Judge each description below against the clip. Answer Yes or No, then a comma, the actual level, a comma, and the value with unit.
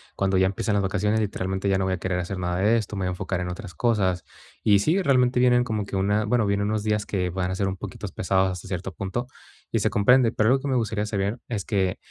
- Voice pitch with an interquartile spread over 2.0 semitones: Yes, average, 2.7 semitones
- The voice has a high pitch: No, low, 100 Hz